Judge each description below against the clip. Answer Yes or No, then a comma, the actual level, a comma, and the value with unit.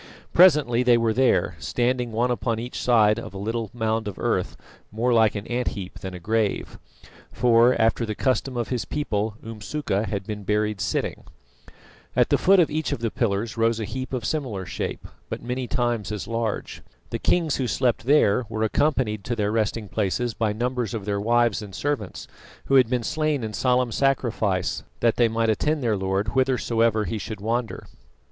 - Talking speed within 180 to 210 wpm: Yes, average, 190 wpm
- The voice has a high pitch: No, low, 115 Hz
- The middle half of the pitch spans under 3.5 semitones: Yes, average, 2.8 semitones